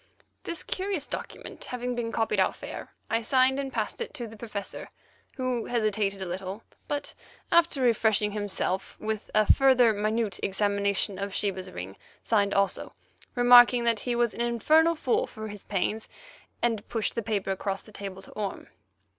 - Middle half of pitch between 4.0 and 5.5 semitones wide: No, average, 3.4 semitones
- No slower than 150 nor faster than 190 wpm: Yes, average, 165 wpm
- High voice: Yes, high, 220 Hz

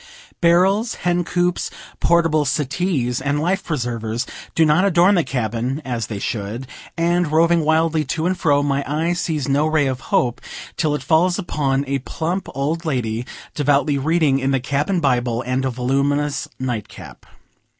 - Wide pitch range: No, average, 4.3 semitones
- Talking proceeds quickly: No, average, 160 wpm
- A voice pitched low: No, medium, 145 Hz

